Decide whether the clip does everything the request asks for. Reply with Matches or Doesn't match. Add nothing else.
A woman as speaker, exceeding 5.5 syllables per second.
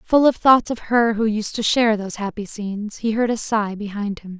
Doesn't match